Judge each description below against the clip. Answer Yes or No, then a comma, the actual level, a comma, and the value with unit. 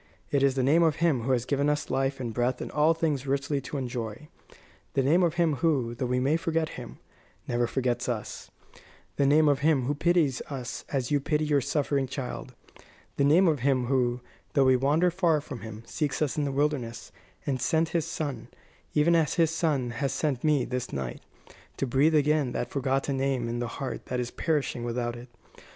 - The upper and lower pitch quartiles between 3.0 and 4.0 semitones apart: Yes, average, 3.3 semitones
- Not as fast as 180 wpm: No, fast, 205 wpm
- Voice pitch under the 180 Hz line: Yes, medium, 140 Hz